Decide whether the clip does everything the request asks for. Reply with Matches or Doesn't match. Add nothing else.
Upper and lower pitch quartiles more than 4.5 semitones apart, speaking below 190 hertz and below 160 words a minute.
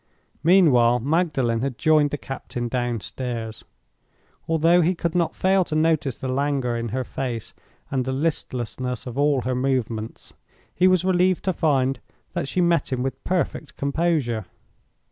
Matches